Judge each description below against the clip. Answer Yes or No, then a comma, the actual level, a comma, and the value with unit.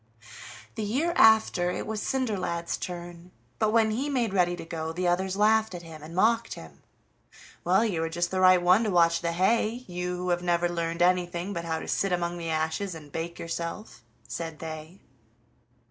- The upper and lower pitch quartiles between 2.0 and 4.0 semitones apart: Yes, average, 3.5 semitones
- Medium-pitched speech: Yes, medium, 175 Hz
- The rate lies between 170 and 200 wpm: Yes, average, 190 wpm